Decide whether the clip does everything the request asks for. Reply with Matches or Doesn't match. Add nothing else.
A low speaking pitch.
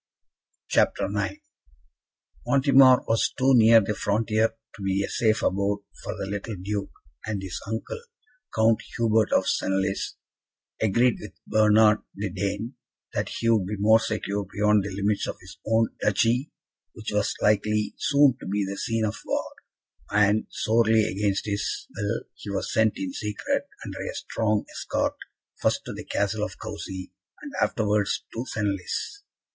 Matches